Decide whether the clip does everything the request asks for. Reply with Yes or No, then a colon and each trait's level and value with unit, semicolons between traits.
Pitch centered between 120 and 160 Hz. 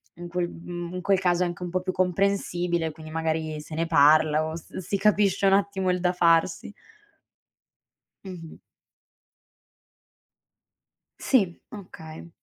No: medium, 175 Hz